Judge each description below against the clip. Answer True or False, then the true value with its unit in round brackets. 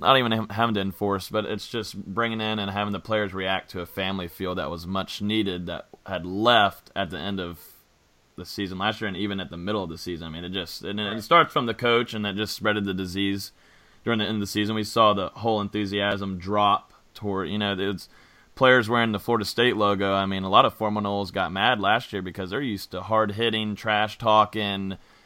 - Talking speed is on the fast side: True (235 wpm)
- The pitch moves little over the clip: True (2.1 semitones)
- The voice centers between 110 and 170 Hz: False (100 Hz)